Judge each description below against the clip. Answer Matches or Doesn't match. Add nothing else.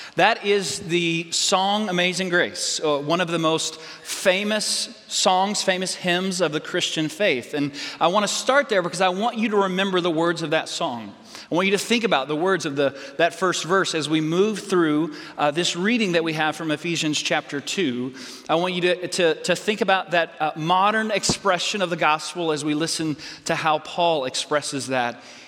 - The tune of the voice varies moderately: Matches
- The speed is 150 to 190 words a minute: Doesn't match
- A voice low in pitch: Doesn't match